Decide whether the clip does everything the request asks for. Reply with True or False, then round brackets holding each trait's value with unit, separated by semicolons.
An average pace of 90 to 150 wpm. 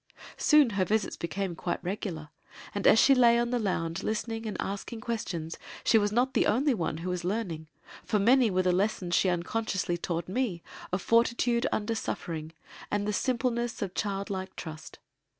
False (175 wpm)